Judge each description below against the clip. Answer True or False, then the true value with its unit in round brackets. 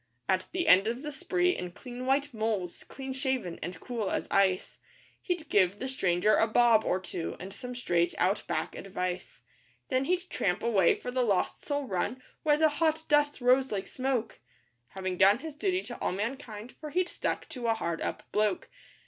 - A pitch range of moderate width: False (6.8 semitones)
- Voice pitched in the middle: False (240 Hz)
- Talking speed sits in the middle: True (190 wpm)